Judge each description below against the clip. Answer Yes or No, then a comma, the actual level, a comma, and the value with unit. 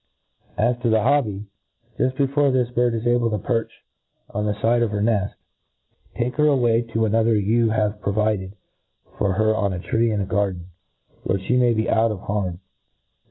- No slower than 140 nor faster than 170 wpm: No, average, 190 wpm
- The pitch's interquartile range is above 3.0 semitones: No, average, 2.7 semitones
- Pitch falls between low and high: No, low, 110 Hz